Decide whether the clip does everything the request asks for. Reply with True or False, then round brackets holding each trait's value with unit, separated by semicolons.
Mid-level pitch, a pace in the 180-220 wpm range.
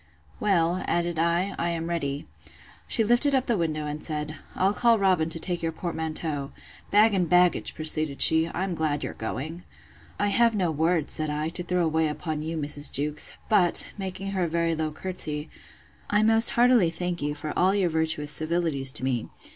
True (165 Hz; 185 wpm)